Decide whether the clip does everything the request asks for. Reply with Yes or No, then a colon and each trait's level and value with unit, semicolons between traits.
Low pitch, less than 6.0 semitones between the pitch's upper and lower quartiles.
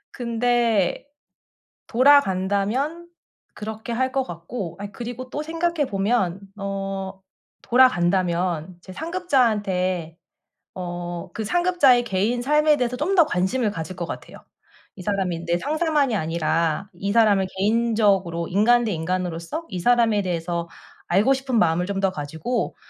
No: high, 200 Hz; wide, 5.6 semitones